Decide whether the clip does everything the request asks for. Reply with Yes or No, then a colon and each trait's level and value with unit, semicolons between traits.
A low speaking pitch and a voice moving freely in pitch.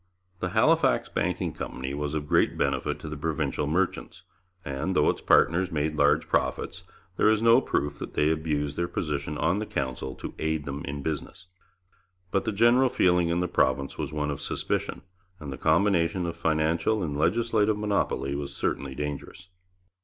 No: very low, 80 Hz; average, 4.4 semitones